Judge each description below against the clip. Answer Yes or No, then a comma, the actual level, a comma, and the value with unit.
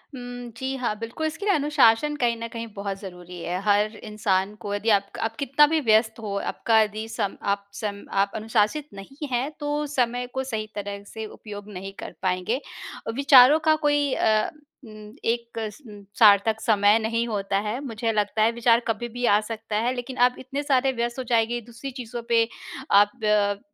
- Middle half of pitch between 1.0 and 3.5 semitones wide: Yes, average, 3.1 semitones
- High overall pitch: Yes, high, 225 Hz